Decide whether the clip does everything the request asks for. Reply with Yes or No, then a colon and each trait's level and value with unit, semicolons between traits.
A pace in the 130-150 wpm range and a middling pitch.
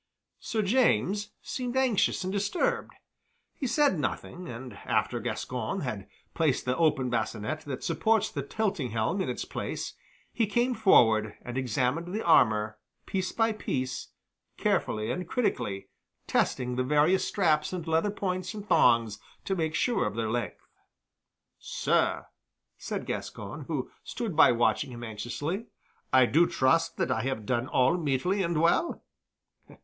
Yes: average, 145 wpm; medium, 155 Hz